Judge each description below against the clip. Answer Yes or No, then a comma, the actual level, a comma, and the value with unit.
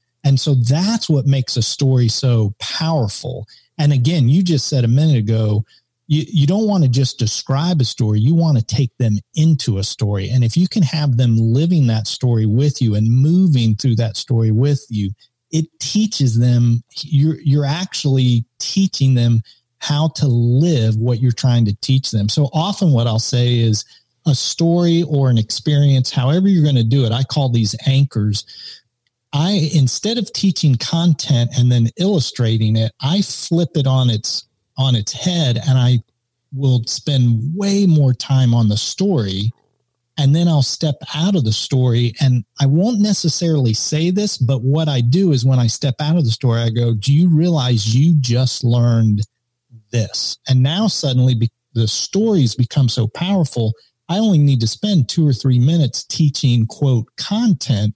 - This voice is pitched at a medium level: No, low, 130 Hz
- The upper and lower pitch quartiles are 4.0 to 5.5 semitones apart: Yes, average, 4.6 semitones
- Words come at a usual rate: Yes, average, 180 wpm